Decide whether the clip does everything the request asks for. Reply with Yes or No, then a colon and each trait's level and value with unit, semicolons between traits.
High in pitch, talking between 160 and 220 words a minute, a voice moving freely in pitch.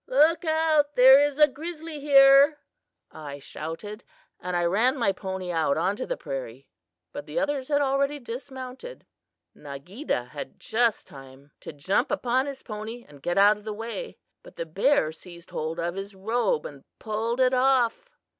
Yes: high, 230 Hz; average, 170 wpm; wide, 8.2 semitones